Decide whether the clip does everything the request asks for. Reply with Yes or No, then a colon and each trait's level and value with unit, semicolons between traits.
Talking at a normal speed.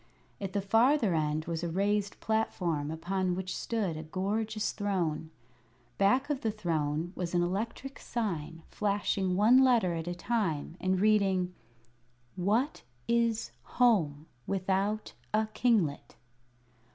No: slow, 125 wpm